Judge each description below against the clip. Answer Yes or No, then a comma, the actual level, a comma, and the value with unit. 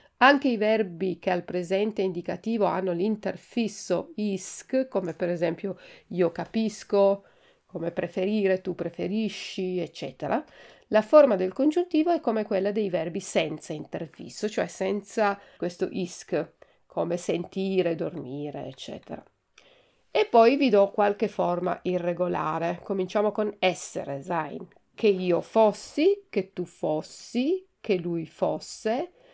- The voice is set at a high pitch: Yes, high, 195 Hz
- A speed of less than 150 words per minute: Yes, average, 120 wpm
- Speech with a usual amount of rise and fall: Yes, average, 3.6 semitones